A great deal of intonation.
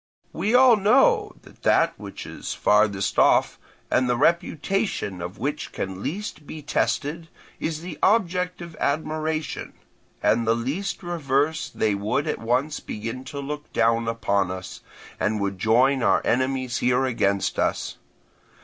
Yes: wide, 6.5 semitones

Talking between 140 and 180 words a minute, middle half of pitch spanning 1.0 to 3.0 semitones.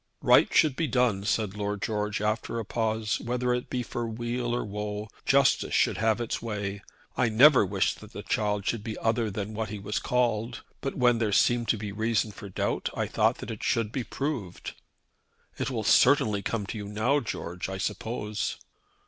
No: average, 195 wpm; narrow, 2.5 semitones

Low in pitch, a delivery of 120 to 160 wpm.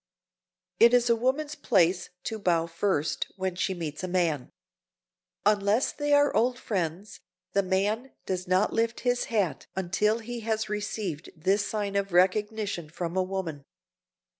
No: high, 200 Hz; average, 150 wpm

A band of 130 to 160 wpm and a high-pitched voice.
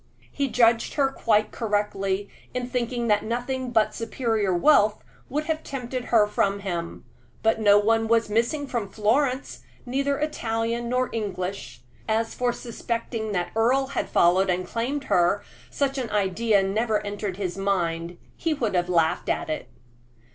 Yes: average, 155 wpm; high, 225 Hz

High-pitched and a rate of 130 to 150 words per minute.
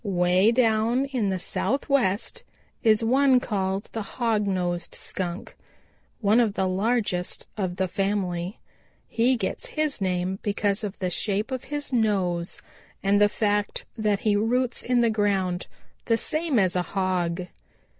Yes: high, 205 Hz; average, 145 wpm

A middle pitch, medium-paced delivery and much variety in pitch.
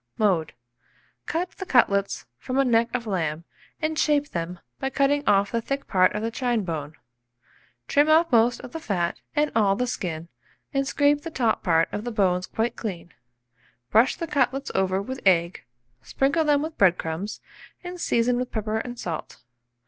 No: high, 230 Hz; average, 180 wpm; wide, 6.7 semitones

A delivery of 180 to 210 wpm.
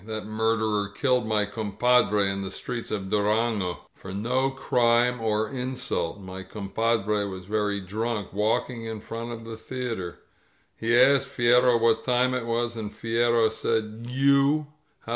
No: average, 150 wpm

